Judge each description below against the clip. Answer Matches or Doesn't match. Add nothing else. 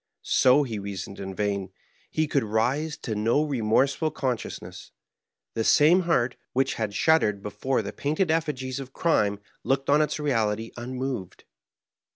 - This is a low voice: Matches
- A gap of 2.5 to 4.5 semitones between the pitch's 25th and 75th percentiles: Doesn't match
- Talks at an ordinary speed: Matches